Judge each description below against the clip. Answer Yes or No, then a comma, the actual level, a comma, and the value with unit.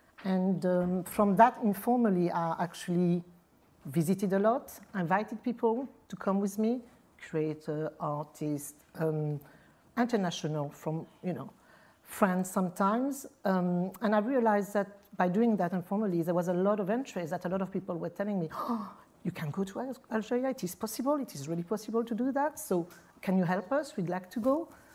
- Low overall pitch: No, high, 195 Hz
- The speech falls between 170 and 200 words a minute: Yes, average, 175 wpm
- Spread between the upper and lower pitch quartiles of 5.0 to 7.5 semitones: No, average, 4.5 semitones